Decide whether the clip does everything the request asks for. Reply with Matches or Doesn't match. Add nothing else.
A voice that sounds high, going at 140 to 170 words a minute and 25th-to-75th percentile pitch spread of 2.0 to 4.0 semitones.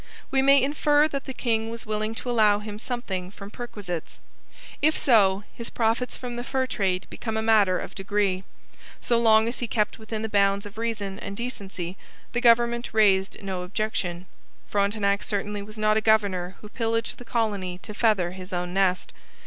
Doesn't match